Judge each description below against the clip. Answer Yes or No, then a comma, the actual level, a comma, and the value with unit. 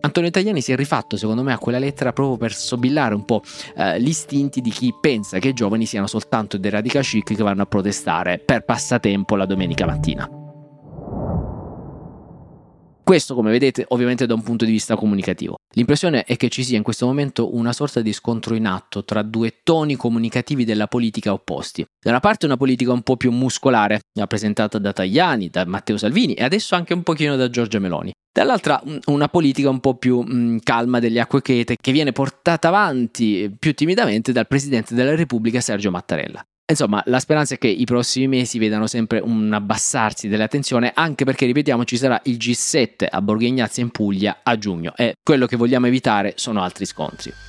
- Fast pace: Yes, fast, 185 wpm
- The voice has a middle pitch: No, low, 120 Hz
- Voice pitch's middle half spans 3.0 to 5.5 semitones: Yes, average, 4.0 semitones